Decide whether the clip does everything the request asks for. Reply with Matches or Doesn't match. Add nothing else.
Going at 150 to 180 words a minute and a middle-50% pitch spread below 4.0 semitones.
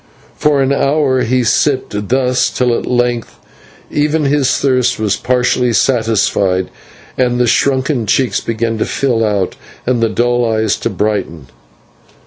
Doesn't match